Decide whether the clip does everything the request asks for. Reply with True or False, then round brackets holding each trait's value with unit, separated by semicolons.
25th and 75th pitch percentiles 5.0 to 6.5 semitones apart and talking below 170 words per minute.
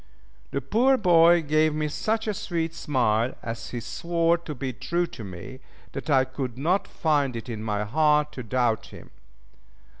False (5.3 semitones; 175 wpm)